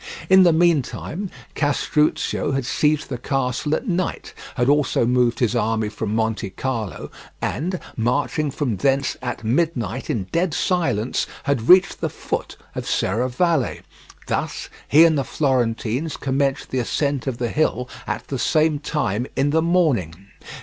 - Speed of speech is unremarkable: Yes, average, 145 wpm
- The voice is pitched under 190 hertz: Yes, low, 135 Hz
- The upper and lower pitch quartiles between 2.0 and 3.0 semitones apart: No, average, 4.6 semitones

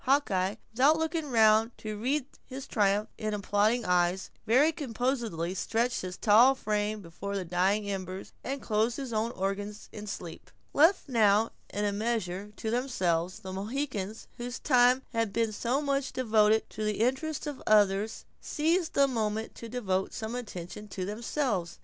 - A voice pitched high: Yes, high, 220 Hz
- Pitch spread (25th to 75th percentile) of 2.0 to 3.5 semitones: No, average, 4.0 semitones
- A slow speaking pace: No, average, 160 wpm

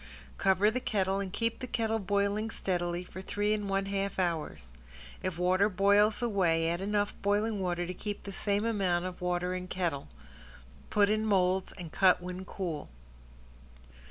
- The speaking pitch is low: No, high, 195 Hz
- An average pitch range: No, narrow, 2.3 semitones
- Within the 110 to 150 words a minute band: No, average, 165 wpm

